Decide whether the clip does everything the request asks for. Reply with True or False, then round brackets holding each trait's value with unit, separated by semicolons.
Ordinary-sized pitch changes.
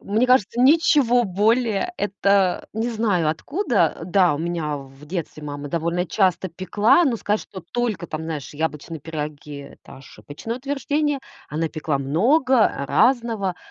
False (7.2 semitones)